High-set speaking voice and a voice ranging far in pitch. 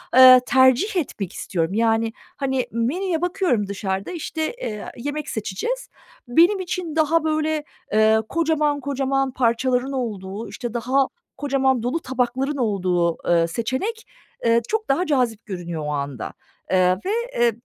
Yes: very high, 255 Hz; wide, 5.9 semitones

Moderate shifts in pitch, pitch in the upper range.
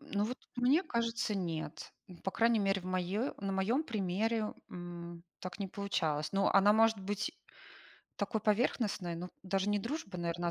Yes: average, 3.8 semitones; high, 195 Hz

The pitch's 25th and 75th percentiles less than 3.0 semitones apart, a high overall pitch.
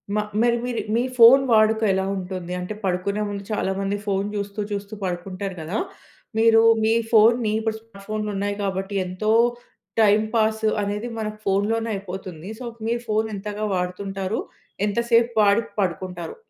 Yes: narrow, 2.4 semitones; high, 205 Hz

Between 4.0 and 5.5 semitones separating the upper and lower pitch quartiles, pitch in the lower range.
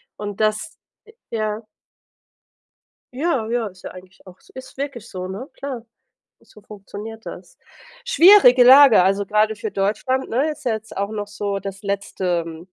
No: average, 4.6 semitones; high, 215 Hz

